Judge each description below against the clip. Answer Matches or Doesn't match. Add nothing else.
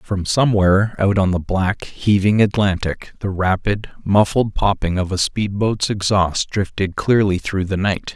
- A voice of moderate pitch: Doesn't match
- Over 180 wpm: Doesn't match